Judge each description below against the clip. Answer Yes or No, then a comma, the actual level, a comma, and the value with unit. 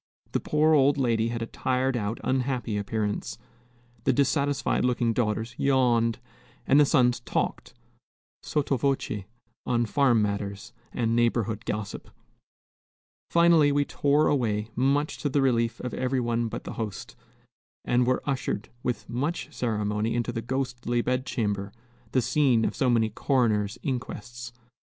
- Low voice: Yes, low, 120 Hz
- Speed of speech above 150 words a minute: No, average, 140 wpm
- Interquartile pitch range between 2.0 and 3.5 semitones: Yes, average, 3.1 semitones